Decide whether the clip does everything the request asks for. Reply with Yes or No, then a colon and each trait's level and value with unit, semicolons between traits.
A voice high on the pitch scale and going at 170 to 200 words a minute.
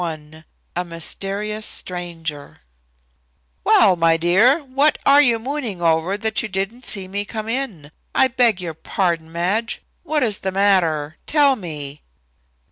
No: high, 195 Hz; average, 140 wpm